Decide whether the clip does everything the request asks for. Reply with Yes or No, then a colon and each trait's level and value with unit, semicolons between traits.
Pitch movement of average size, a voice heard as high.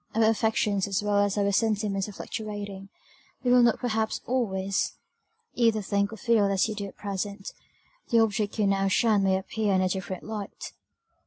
No: narrow, 2.0 semitones; high, 205 Hz